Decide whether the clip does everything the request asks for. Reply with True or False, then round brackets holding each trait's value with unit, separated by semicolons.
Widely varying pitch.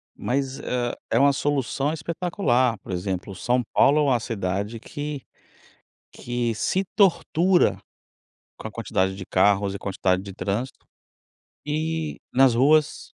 True (6.7 semitones)